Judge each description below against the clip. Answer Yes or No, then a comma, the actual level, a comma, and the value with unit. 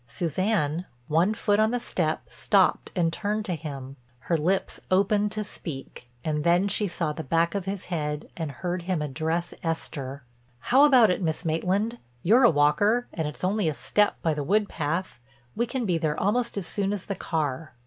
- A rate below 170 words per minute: No, average, 190 wpm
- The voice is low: No, medium, 175 Hz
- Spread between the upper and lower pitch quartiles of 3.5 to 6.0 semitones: Yes, average, 4.8 semitones